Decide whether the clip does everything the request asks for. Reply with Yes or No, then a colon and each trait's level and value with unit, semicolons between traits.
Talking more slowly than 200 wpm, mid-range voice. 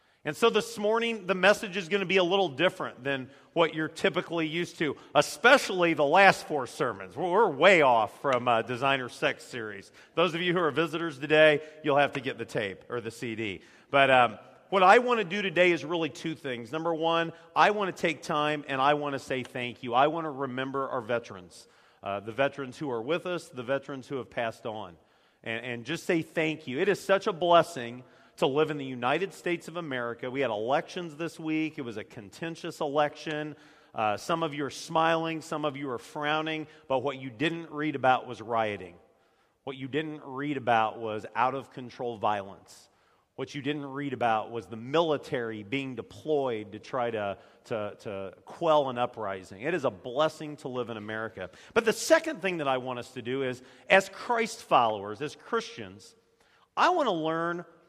No: fast, 205 wpm; medium, 150 Hz